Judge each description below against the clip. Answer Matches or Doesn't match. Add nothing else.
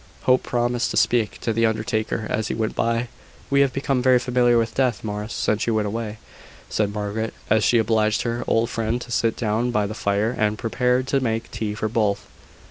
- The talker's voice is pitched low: Matches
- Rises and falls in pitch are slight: Matches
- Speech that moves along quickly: Matches